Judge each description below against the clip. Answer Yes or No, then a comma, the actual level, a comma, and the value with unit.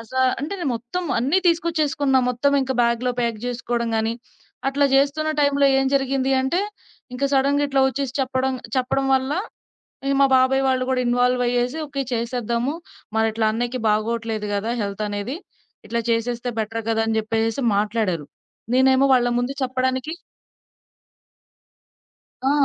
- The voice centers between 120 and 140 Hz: No, very high, 250 Hz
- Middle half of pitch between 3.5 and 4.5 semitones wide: No, average, 3.0 semitones